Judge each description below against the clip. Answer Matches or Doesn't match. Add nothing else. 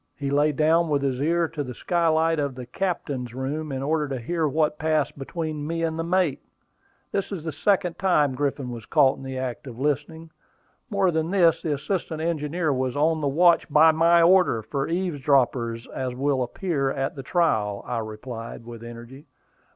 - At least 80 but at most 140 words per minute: Doesn't match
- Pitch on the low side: Doesn't match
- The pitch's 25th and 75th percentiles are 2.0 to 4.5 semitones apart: Matches